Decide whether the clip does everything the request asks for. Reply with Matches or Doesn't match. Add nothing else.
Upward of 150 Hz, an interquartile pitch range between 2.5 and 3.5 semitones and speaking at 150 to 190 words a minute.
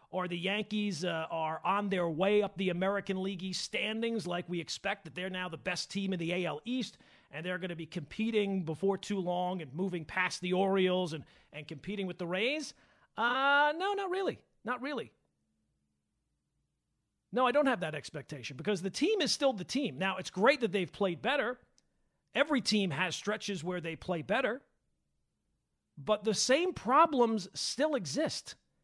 Doesn't match